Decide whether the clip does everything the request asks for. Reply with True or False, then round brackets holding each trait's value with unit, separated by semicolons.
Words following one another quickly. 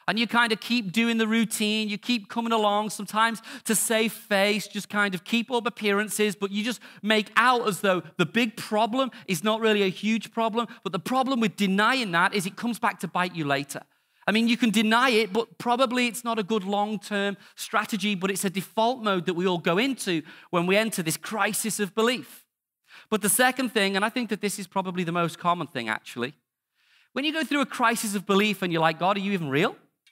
True (230 wpm)